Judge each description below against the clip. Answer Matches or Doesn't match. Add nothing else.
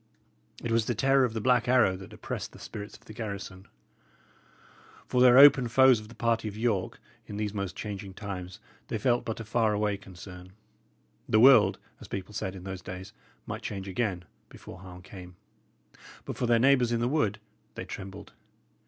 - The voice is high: Doesn't match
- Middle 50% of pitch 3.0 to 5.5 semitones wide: Matches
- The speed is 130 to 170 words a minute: Doesn't match